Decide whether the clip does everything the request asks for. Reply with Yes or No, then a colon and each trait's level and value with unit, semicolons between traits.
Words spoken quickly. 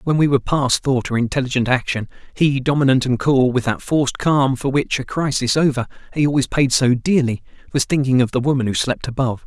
Yes: fast, 215 wpm